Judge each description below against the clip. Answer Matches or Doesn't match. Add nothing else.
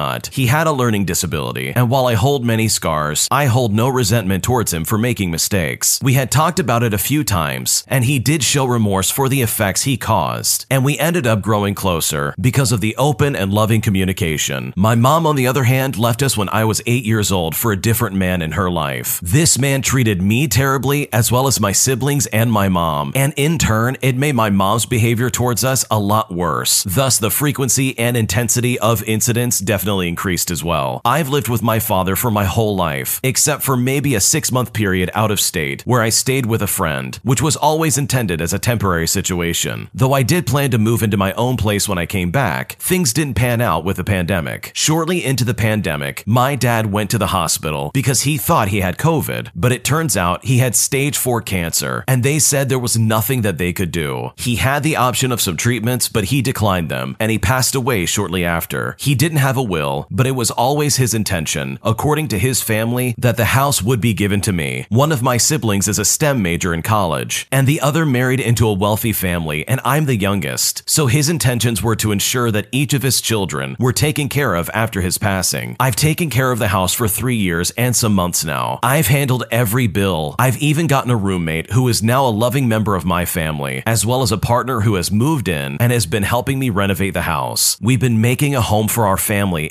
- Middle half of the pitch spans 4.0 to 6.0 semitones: Matches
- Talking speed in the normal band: Doesn't match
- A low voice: Matches